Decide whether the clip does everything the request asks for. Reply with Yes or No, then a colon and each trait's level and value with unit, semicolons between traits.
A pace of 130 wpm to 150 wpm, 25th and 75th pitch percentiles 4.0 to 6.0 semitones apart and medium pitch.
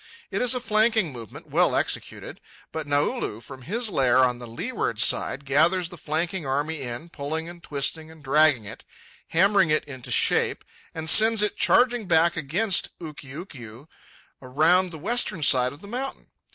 No: average, 165 wpm; wide, 5.6 semitones; medium, 160 Hz